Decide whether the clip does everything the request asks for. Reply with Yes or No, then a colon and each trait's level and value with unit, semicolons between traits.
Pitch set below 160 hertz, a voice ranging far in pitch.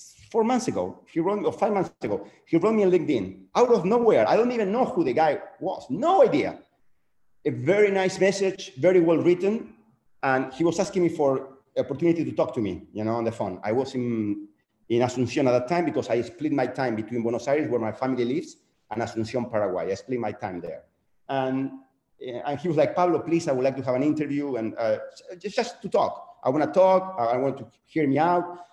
Yes: medium, 140 Hz; wide, 7.1 semitones